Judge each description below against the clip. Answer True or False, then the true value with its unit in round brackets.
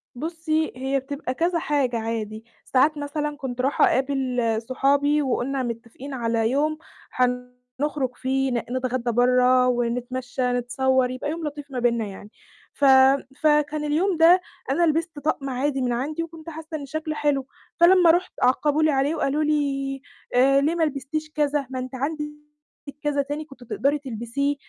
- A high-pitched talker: True (275 Hz)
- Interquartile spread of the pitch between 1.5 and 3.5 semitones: True (3.1 semitones)